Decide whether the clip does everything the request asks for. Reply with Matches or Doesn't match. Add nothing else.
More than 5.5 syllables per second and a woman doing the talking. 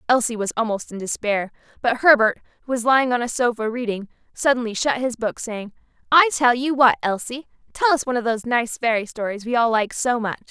Matches